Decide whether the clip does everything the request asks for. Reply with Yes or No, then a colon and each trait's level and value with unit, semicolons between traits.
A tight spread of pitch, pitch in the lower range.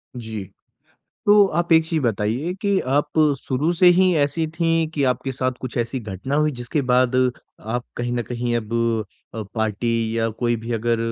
No: average, 5.1 semitones; low, 125 Hz